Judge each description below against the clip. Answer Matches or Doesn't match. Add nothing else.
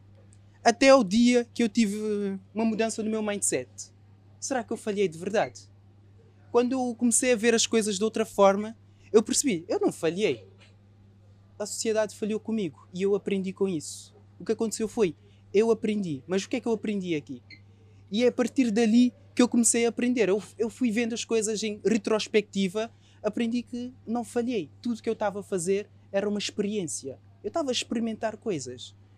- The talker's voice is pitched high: Matches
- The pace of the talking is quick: Matches